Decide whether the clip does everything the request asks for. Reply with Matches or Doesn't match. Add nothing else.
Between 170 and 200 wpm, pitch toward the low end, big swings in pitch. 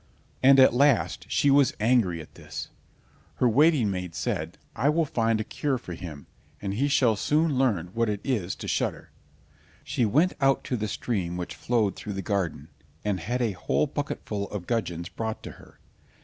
Matches